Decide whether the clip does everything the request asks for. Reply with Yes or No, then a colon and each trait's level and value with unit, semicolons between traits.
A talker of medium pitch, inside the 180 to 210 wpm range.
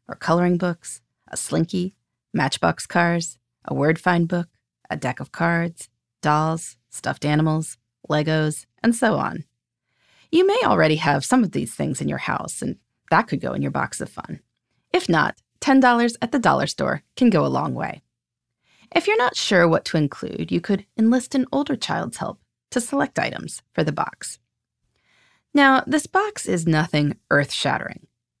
No: medium, 170 Hz; average, 170 wpm